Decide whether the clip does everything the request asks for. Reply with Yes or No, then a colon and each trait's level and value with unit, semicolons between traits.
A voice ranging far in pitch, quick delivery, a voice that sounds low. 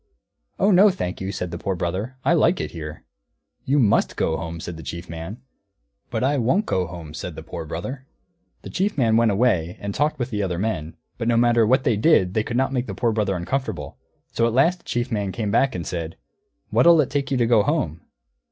Yes: wide, 6.8 semitones; fast, 225 wpm; low, 110 Hz